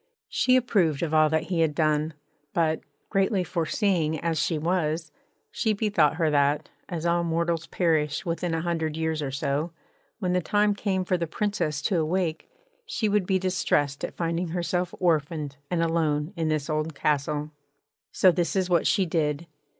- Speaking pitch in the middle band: Yes, medium, 165 Hz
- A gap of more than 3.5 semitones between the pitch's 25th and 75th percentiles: No, average, 2.9 semitones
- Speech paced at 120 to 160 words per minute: No, average, 175 wpm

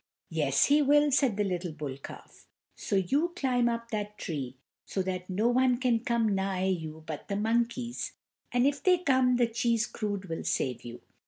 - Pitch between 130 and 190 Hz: No, high, 225 Hz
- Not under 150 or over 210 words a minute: Yes, average, 185 wpm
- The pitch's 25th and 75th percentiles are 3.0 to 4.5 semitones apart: No, average, 5.2 semitones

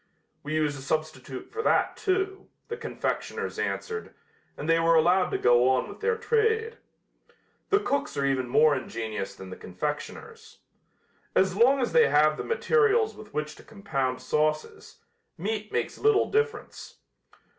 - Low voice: No, medium, 165 Hz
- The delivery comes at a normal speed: Yes, average, 155 wpm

